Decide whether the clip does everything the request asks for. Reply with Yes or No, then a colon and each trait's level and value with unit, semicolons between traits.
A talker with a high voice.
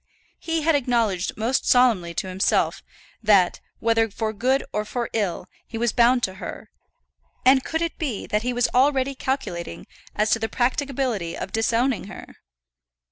Yes: high, 235 Hz